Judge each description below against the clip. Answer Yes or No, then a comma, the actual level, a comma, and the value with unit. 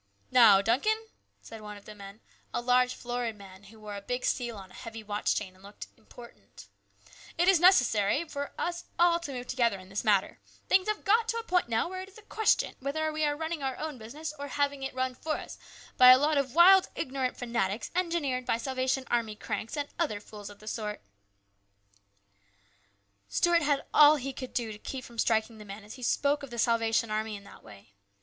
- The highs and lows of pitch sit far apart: Yes, wide, 5.7 semitones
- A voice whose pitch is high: Yes, very high, 250 Hz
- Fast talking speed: Yes, fast, 220 wpm